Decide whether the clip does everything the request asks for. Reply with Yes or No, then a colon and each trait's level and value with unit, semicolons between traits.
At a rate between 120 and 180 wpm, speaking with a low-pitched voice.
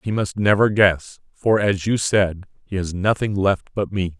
No: average, 200 wpm; low, 100 Hz